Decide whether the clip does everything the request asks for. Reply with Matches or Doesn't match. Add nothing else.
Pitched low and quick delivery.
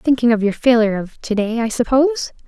Doesn't match